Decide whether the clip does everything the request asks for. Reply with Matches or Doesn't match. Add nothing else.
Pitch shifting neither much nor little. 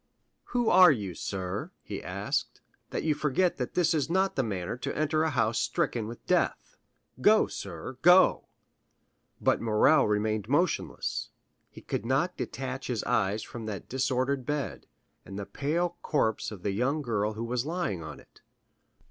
Doesn't match